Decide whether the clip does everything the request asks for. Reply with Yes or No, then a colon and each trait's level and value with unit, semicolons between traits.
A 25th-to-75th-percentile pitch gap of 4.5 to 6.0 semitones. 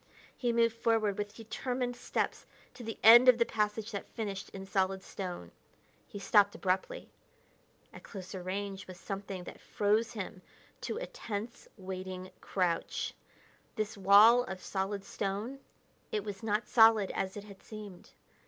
No: average, 2.9 semitones